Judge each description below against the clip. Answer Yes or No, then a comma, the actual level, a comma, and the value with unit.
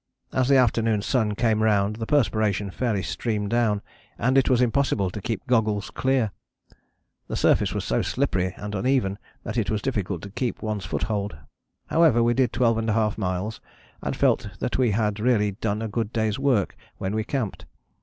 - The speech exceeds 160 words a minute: Yes, average, 175 wpm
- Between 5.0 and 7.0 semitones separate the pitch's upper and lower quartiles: No, average, 2.8 semitones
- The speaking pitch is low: Yes, low, 110 Hz